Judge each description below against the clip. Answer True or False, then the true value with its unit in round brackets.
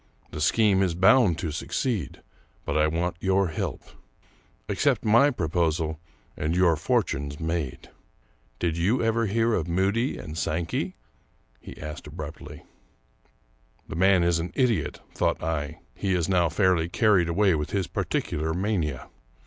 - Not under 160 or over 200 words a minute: False (140 wpm)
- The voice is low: True (85 Hz)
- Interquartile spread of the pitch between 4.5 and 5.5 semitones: False (3.7 semitones)